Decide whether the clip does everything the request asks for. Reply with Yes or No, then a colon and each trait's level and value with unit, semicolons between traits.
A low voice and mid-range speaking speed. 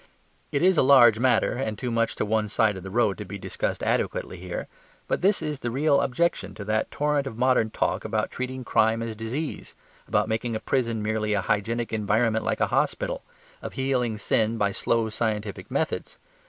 Yes: low, 115 Hz; average, 195 wpm